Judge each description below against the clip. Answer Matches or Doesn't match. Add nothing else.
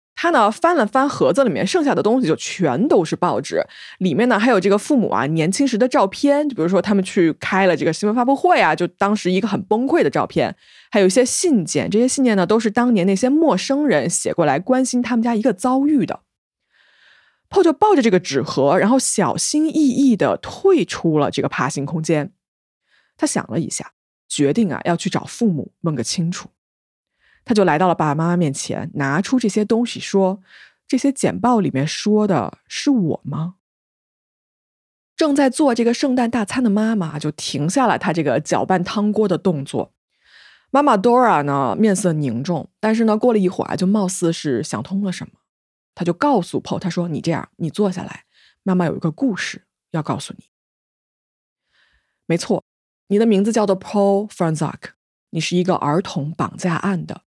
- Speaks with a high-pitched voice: Matches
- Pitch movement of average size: Doesn't match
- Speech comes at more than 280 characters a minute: Matches